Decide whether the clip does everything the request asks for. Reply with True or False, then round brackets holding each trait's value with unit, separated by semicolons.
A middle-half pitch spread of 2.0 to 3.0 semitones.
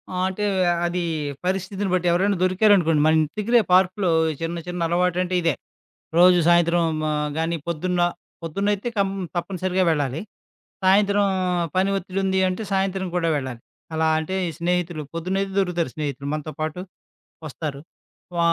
True (2.5 semitones)